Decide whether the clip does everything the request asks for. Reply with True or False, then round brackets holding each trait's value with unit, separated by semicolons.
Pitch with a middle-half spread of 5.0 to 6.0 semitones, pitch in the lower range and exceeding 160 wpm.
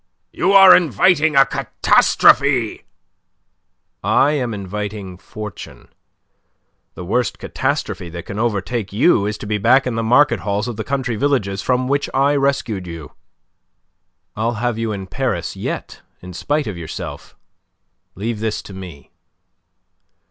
False (5.3 semitones; 110 Hz; 140 wpm)